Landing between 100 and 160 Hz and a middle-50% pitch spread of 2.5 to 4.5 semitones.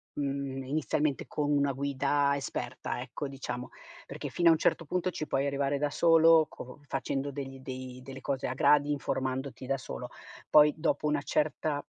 No: medium, 140 Hz; narrow, 1.8 semitones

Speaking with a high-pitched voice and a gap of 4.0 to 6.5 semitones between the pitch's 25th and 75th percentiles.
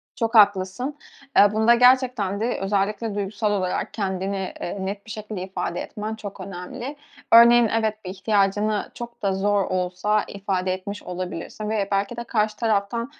No: high, 205 Hz; narrow, 2.4 semitones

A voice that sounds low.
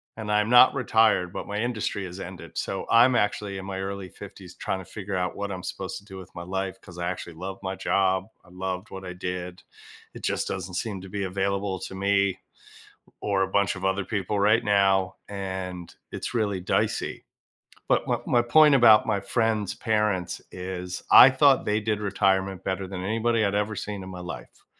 Yes: very low, 95 Hz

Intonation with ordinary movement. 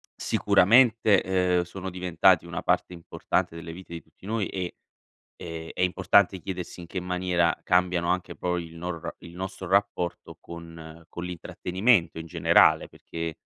No: narrow, 1.8 semitones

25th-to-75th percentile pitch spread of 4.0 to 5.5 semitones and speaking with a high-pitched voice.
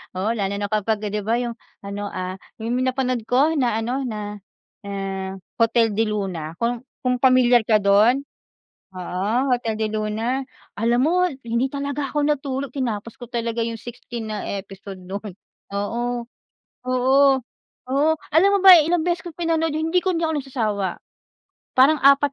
Yes: average, 4.4 semitones; high, 235 Hz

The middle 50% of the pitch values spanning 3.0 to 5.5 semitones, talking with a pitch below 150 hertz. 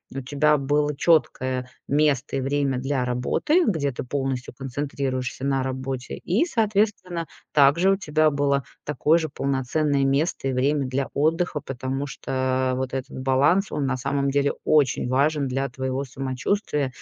No: narrow, 2.4 semitones; medium, 140 Hz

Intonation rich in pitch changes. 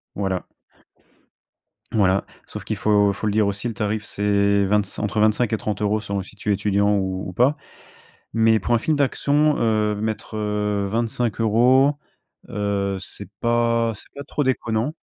No: narrow, 2.5 semitones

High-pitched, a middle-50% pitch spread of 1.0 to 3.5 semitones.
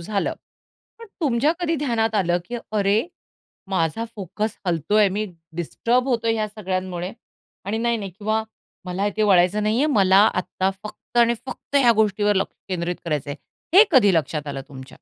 No: high, 205 Hz; average, 3.9 semitones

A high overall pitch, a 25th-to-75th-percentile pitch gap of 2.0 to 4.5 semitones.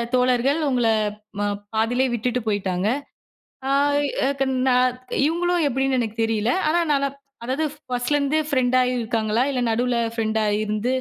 Yes: very high, 250 Hz; average, 3.5 semitones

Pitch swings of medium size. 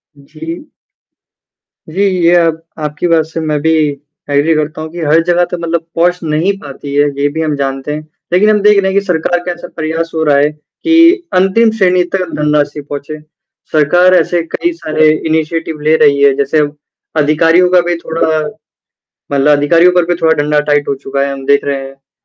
Yes: average, 3.2 semitones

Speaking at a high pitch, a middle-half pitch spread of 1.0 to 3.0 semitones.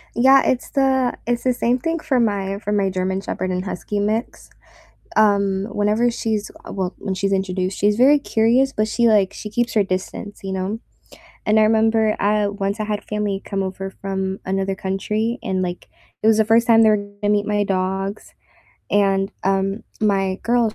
Yes: high, 205 Hz; narrow, 2.5 semitones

